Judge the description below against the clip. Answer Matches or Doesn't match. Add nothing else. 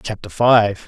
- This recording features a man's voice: Matches